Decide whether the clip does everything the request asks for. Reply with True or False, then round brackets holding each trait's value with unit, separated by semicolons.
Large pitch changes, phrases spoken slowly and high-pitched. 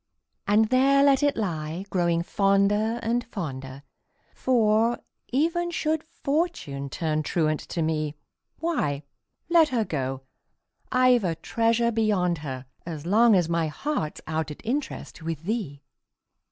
True (8.0 semitones; 130 wpm; 200 Hz)